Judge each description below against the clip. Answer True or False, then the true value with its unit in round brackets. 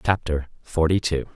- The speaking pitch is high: False (80 Hz)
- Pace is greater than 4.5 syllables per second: True (4.9 syllables/s)